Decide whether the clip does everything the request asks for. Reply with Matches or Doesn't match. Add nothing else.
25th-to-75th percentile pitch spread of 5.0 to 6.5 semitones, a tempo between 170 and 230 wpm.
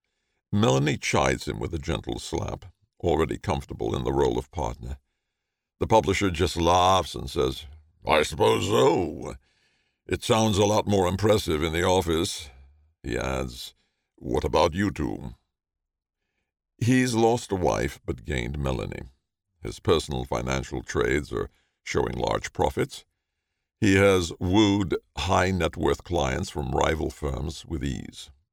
Doesn't match